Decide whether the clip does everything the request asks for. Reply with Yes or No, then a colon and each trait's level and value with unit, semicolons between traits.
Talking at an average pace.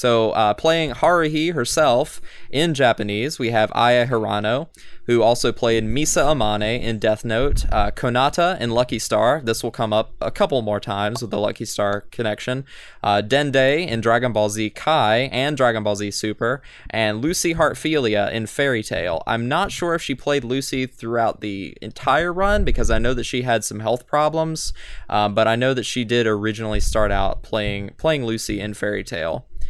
Yes: average, 185 wpm